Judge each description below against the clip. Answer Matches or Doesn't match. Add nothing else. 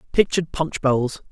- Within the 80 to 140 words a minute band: Matches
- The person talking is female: Doesn't match